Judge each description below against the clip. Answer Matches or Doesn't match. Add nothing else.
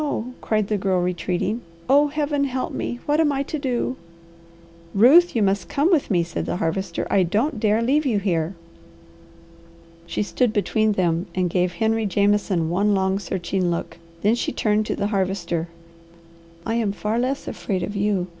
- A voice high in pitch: Matches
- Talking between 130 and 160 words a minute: Doesn't match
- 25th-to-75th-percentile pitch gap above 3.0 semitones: Matches